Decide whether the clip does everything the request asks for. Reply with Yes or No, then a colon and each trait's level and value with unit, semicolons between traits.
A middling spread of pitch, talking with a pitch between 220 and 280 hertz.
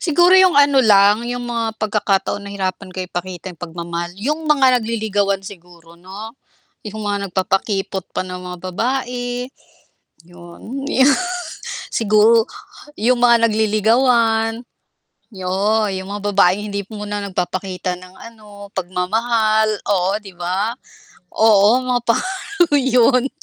No: average, 3.6 semitones; high, 210 Hz